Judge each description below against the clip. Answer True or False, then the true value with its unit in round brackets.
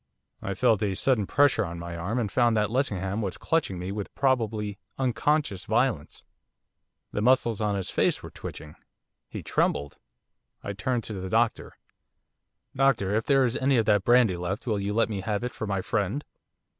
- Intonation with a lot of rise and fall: False (4.1 semitones)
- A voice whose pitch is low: True (105 Hz)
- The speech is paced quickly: False (180 wpm)